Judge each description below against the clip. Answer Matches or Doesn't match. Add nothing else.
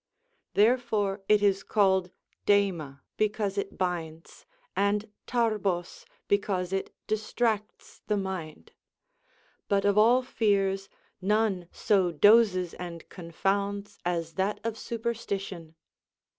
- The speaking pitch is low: Doesn't match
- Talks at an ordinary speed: Doesn't match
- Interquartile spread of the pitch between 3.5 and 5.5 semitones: Doesn't match